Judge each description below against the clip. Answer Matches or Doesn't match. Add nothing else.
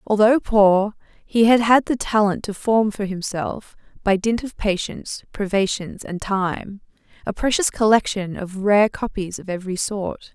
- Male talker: Doesn't match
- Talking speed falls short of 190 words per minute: Matches